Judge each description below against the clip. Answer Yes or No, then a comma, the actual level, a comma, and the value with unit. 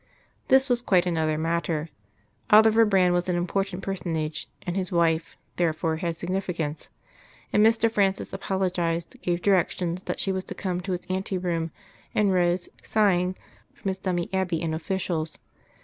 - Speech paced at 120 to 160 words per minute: Yes, average, 155 wpm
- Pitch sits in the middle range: Yes, medium, 180 Hz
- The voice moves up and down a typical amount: No, narrow, 2.3 semitones